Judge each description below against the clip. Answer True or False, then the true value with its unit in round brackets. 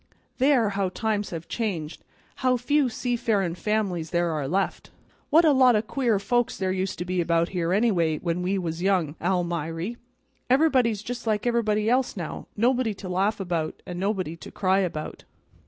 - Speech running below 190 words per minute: True (170 wpm)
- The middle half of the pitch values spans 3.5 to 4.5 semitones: False (5.1 semitones)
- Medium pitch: False (195 Hz)